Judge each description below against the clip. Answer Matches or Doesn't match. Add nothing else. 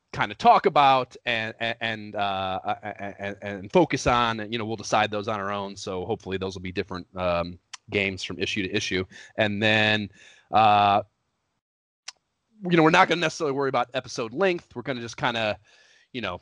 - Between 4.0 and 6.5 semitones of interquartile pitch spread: Doesn't match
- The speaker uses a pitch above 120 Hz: Doesn't match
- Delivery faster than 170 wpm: Matches